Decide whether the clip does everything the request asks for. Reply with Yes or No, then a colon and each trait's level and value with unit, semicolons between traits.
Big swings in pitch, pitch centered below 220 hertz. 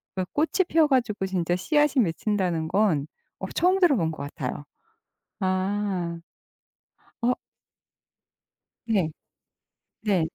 Yes: wide, 6.5 semitones; high, 190 Hz